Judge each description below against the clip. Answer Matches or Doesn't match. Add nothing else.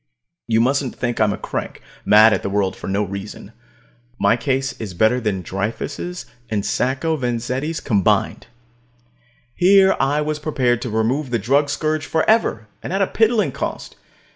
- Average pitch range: Doesn't match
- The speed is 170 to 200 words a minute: Doesn't match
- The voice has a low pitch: Matches